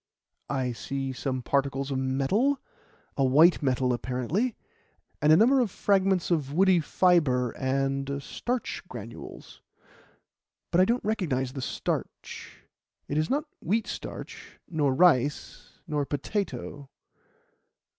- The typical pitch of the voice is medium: Yes, medium, 145 Hz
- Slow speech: Yes, slow, 120 wpm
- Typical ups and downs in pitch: No, wide, 6.0 semitones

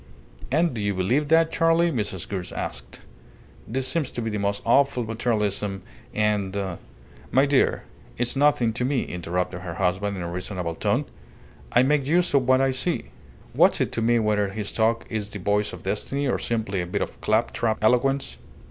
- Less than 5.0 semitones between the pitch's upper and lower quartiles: No, average, 5.3 semitones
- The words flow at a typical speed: Yes, average, 185 wpm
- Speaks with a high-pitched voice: No, low, 110 Hz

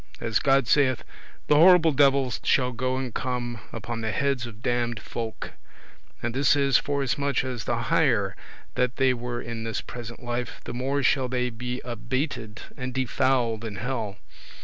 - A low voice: Yes, low, 125 Hz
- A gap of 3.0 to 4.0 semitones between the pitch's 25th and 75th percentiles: No, narrow, 2.4 semitones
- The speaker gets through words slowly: No, average, 170 wpm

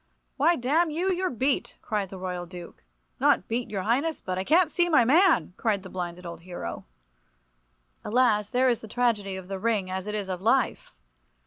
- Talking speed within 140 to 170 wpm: No, average, 195 wpm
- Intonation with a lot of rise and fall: Yes, wide, 6.1 semitones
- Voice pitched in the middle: No, high, 215 Hz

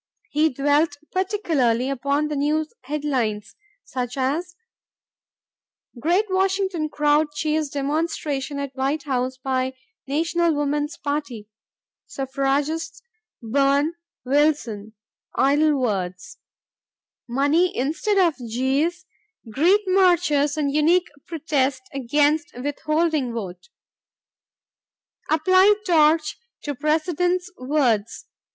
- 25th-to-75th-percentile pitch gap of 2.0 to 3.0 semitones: No, average, 3.5 semitones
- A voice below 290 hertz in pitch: No, very high, 295 Hz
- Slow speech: Yes, slow, 90 wpm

